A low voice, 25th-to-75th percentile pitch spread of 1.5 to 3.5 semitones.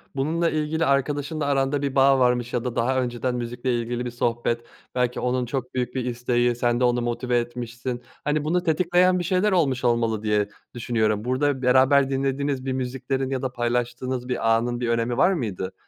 Yes: low, 125 Hz; narrow, 2.4 semitones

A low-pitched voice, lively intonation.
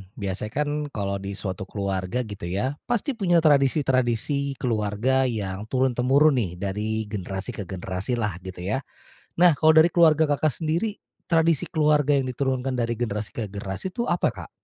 Yes: low, 125 Hz; wide, 6.7 semitones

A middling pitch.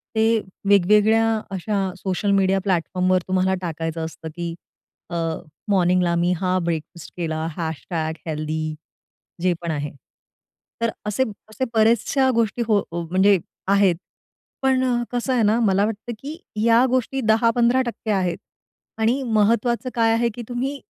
No: high, 200 Hz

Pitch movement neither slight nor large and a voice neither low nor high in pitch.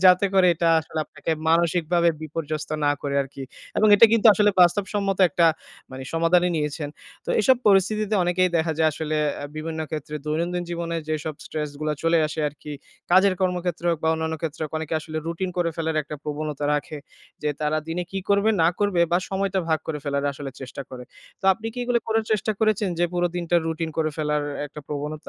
Yes: average, 3.1 semitones; medium, 165 Hz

